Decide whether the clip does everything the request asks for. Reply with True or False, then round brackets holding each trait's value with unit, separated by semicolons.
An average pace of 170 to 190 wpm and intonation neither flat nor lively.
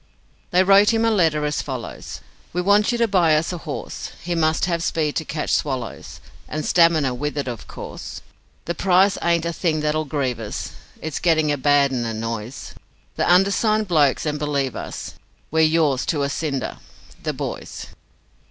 True (180 wpm; 3.7 semitones)